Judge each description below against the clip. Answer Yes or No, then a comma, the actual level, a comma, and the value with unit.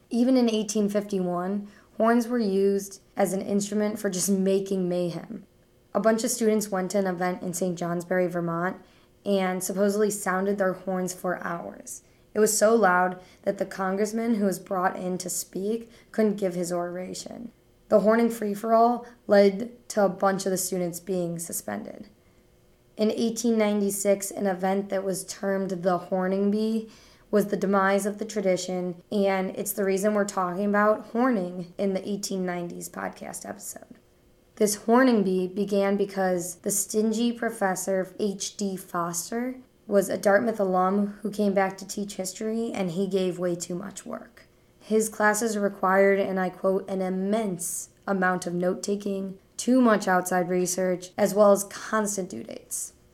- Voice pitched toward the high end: Yes, high, 195 Hz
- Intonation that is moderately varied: No, narrow, 2.3 semitones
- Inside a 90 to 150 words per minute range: No, average, 160 wpm